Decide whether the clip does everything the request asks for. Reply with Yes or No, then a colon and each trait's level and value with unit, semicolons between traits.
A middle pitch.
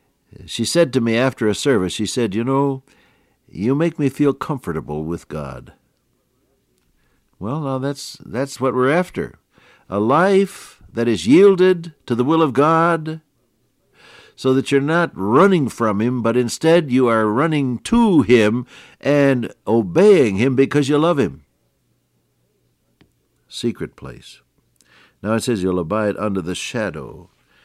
No: low, 130 Hz